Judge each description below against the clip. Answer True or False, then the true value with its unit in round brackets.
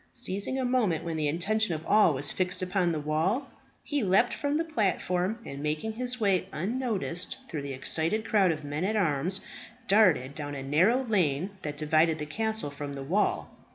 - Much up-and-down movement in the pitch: True (6.2 semitones)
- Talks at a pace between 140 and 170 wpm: False (190 wpm)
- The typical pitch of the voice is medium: True (180 Hz)